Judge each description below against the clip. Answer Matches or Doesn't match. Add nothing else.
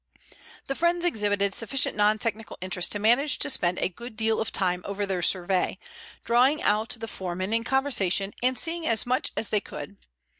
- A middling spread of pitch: Matches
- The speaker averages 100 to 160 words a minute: Doesn't match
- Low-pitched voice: Doesn't match